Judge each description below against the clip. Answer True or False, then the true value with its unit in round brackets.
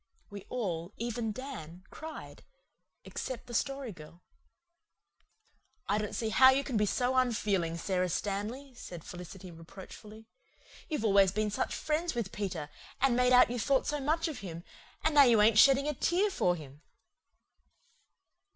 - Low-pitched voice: False (220 Hz)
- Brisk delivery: False (155 wpm)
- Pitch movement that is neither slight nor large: False (5.9 semitones)